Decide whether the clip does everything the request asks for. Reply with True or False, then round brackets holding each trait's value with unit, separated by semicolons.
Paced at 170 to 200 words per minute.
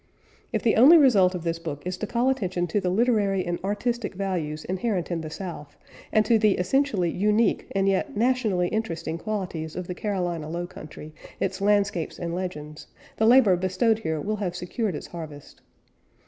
True (180 wpm)